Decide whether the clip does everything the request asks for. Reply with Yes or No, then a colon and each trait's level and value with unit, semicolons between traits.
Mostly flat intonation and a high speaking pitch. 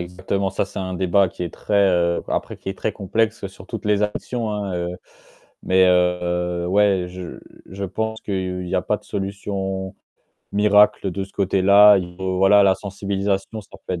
No: narrow, 1.9 semitones; very low, 95 Hz